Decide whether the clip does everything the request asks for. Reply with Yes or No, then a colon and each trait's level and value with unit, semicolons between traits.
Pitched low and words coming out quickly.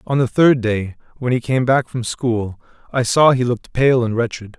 Yes: low, 120 Hz; fast, 225 wpm